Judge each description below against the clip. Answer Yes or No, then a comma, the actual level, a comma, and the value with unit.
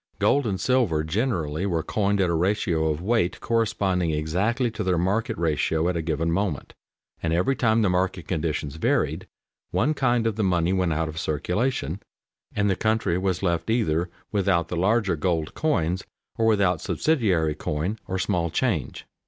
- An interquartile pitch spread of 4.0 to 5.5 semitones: Yes, average, 4.7 semitones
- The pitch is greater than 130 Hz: No, very low, 90 Hz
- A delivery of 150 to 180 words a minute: Yes, average, 170 wpm